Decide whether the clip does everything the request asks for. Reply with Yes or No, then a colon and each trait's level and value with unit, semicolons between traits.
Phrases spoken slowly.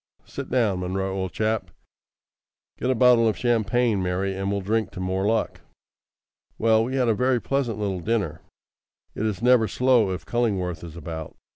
No: average, 170 wpm